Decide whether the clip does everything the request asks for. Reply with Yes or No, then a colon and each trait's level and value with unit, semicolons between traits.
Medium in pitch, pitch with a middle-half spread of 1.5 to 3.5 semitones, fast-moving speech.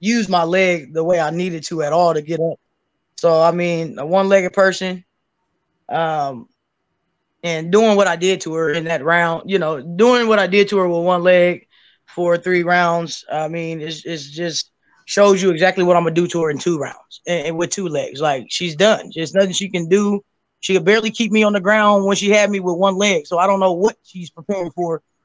Yes: medium, 180 Hz; average, 2.9 semitones; fast, 235 wpm